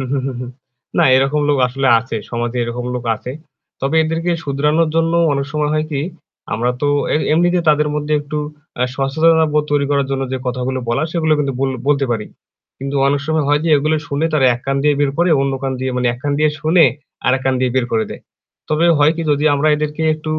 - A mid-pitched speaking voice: Yes, medium, 145 Hz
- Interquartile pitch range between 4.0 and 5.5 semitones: No, narrow, 2.6 semitones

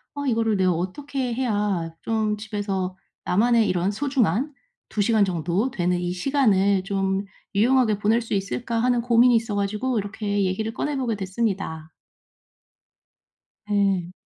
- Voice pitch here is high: Yes, high, 210 Hz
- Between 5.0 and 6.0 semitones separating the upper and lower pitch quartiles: No, average, 3.5 semitones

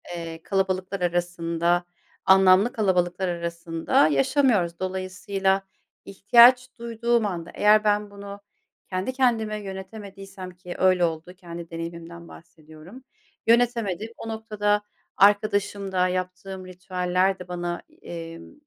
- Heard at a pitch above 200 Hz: No, medium, 185 Hz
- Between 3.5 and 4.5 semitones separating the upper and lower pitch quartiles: No, average, 3.0 semitones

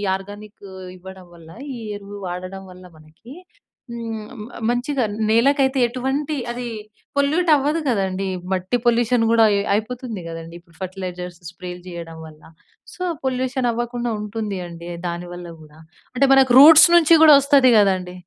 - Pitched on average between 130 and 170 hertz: No, high, 215 Hz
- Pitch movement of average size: No, wide, 5.9 semitones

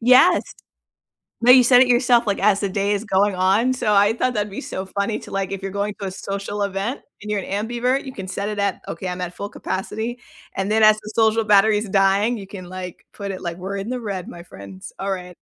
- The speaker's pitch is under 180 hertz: No, high, 200 Hz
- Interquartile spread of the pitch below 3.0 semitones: Yes, narrow, 2.5 semitones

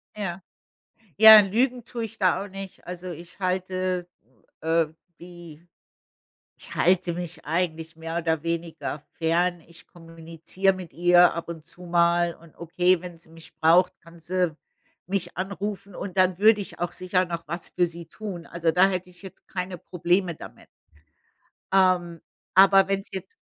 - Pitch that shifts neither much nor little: No, narrow, 1.9 semitones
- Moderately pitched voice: Yes, medium, 175 Hz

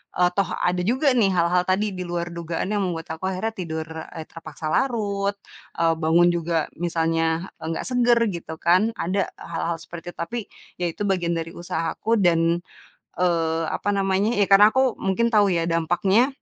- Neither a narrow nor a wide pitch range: Yes, average, 3.4 semitones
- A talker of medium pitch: Yes, medium, 175 Hz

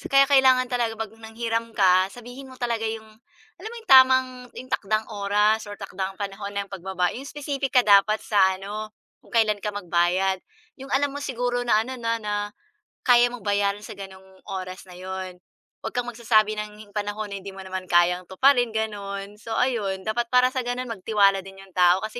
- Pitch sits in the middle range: No, high, 215 Hz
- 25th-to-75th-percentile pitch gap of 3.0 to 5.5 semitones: Yes, average, 3.9 semitones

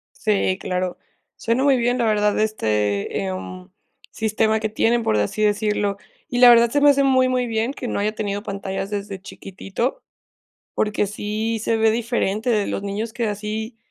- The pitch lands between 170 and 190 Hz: No, high, 215 Hz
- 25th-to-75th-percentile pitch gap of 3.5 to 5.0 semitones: No, average, 2.8 semitones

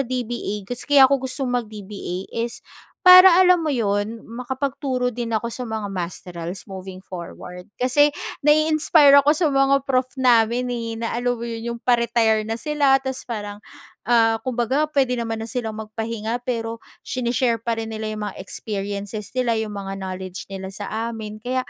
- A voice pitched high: Yes, high, 230 Hz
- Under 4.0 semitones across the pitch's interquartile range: Yes, average, 3.3 semitones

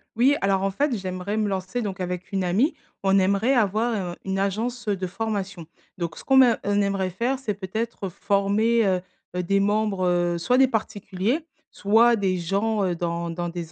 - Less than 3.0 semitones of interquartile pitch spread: No, average, 3.3 semitones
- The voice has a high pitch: Yes, high, 200 Hz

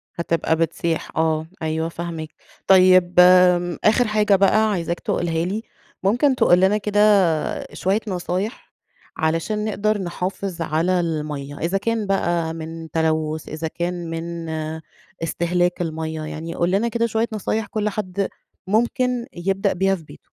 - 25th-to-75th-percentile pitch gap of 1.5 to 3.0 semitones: No, average, 3.8 semitones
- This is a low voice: No, medium, 180 Hz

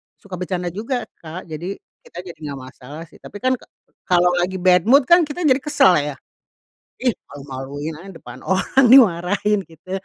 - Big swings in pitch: Yes, wide, 6.4 semitones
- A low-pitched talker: No, medium, 180 Hz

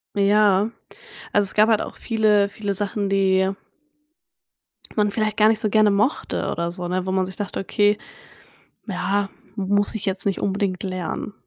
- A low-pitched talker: No, high, 200 Hz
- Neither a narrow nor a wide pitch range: No, narrow, 1.8 semitones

